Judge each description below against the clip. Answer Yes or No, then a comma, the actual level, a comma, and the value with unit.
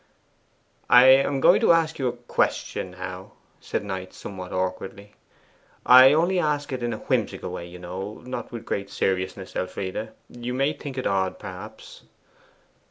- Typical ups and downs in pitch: No, wide, 6.0 semitones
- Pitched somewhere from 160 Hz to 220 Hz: No, low, 120 Hz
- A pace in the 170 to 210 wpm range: No, average, 160 wpm